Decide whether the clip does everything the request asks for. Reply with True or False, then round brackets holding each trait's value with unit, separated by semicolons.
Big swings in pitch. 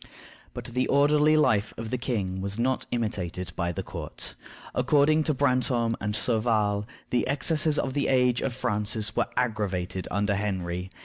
False (4.4 semitones)